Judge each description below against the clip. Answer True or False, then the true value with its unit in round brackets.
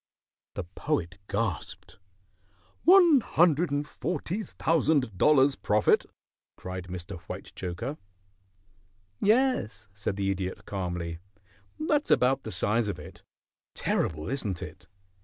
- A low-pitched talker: True (115 Hz)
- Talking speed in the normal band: False (105 wpm)